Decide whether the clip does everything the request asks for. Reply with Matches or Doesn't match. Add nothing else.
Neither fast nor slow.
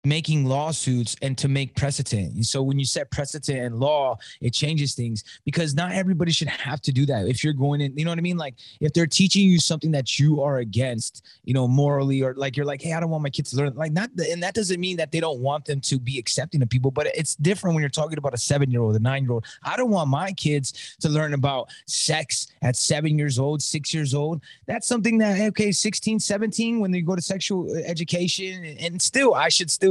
Doesn't match